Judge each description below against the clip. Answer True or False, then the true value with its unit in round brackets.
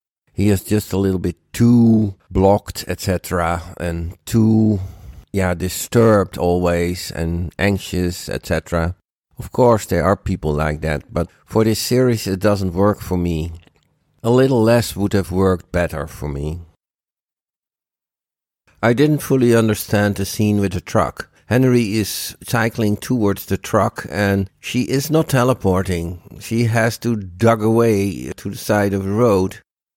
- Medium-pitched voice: False (100 Hz)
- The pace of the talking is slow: False (145 wpm)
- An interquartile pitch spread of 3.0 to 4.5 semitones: True (4.1 semitones)